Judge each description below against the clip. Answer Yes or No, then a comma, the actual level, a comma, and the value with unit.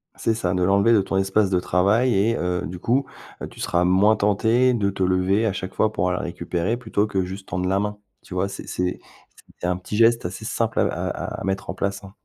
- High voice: No, low, 100 Hz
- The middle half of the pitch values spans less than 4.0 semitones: Yes, average, 3.0 semitones